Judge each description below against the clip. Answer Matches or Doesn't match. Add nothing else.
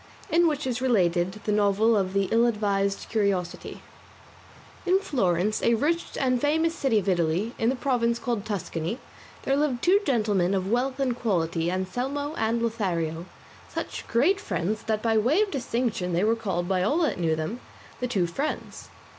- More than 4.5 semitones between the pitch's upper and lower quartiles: Matches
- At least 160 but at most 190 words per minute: Matches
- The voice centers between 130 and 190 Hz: Doesn't match